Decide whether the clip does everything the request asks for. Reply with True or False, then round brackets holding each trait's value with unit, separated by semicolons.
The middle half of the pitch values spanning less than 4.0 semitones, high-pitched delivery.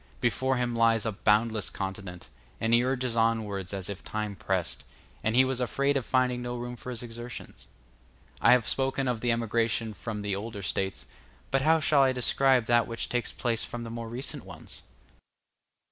False (2.6 semitones; 115 Hz)